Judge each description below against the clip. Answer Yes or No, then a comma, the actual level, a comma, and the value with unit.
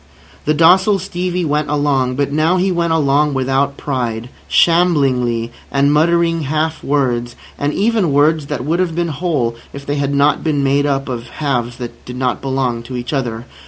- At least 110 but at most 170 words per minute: No, average, 180 wpm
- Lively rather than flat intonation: No, average, 4.0 semitones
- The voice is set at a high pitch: No, medium, 145 Hz